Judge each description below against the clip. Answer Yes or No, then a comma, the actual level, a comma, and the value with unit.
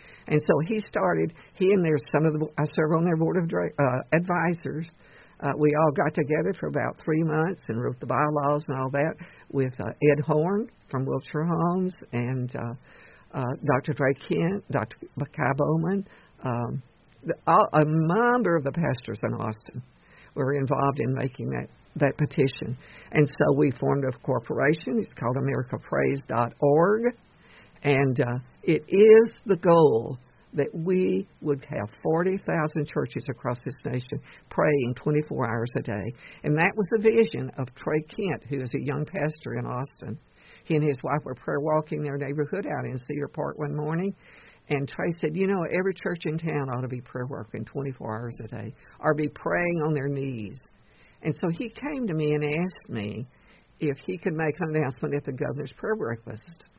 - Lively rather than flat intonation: No, average, 3.5 semitones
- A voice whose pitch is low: No, medium, 150 Hz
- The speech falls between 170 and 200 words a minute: Yes, average, 180 wpm